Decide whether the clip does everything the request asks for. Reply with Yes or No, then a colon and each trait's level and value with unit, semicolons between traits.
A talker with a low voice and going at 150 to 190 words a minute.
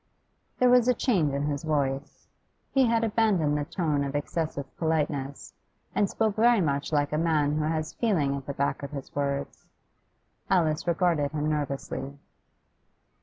No: medium, 150 Hz; average, 160 wpm